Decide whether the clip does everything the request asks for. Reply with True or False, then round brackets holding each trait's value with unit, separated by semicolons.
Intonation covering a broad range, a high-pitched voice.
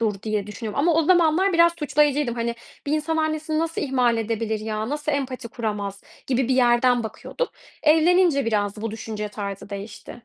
True (6.0 semitones; 245 Hz)